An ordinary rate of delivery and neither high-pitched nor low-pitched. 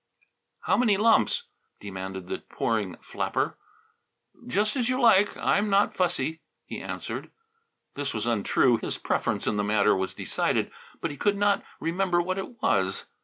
Yes: average, 155 wpm; medium, 165 Hz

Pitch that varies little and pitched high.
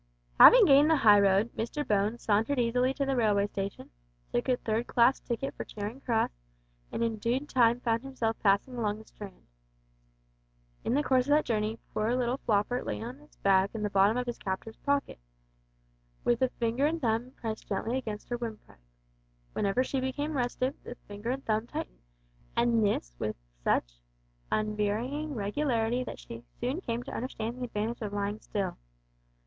No: average, 3.4 semitones; high, 230 Hz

